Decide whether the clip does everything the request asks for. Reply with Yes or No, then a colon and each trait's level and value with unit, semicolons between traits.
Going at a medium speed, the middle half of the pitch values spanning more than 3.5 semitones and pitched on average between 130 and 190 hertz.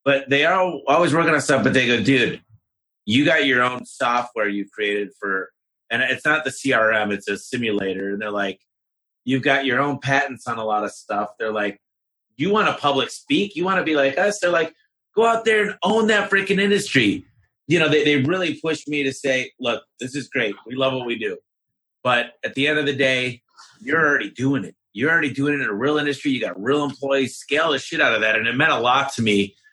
No: fast, 235 wpm; average, 5.0 semitones; low, 135 Hz